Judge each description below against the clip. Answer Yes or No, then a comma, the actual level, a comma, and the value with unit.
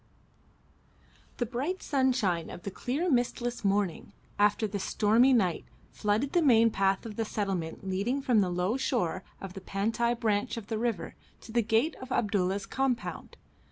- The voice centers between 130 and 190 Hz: No, high, 220 Hz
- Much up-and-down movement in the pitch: No, average, 3.8 semitones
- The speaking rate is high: No, average, 160 wpm